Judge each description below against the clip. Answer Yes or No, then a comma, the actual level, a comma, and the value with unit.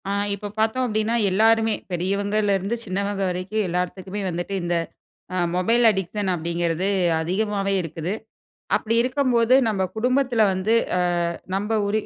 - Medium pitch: No, high, 200 Hz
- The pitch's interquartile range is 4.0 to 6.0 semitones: No, average, 3.3 semitones